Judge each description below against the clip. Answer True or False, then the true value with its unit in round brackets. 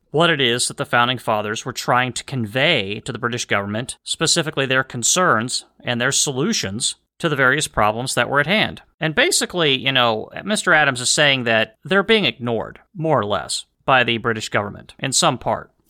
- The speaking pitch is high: False (130 Hz)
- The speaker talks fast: False (195 wpm)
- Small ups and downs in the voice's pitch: False (5.2 semitones)